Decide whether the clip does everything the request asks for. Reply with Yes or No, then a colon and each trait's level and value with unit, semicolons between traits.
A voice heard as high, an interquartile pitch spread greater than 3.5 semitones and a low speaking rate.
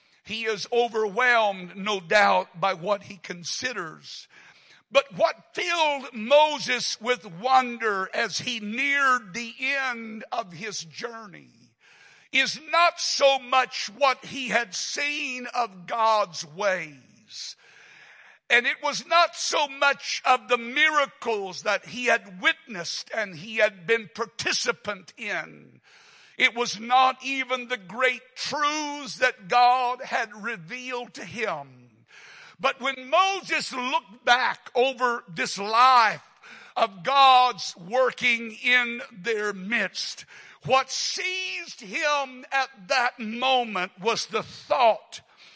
Yes: high, 245 Hz; average, 4.2 semitones; slow, 115 wpm